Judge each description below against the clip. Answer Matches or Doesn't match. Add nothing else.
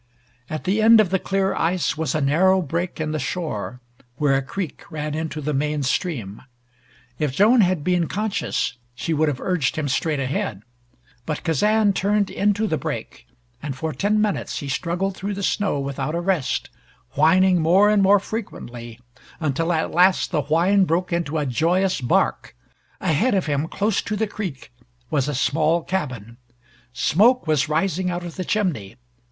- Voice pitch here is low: Doesn't match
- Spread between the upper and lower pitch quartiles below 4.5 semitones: Doesn't match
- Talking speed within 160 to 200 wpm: Matches